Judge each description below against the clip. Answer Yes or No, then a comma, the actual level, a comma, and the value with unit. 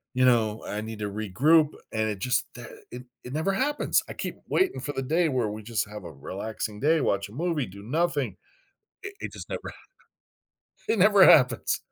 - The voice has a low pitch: Yes, low, 125 Hz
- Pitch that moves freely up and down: Yes, wide, 7.1 semitones